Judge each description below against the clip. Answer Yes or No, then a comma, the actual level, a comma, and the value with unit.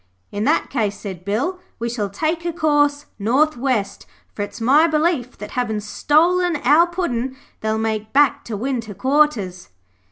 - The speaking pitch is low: No, very high, 255 Hz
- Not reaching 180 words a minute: Yes, average, 160 wpm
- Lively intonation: Yes, wide, 5.9 semitones